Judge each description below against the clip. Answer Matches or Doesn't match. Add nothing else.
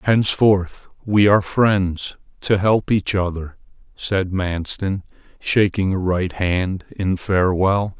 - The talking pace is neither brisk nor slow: Doesn't match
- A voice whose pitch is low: Matches